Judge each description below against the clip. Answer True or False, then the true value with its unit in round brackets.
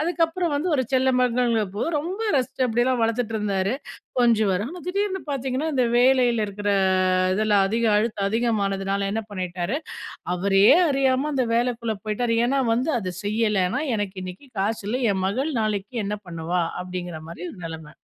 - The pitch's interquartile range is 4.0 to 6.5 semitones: True (4.7 semitones)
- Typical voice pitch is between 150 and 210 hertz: False (225 Hz)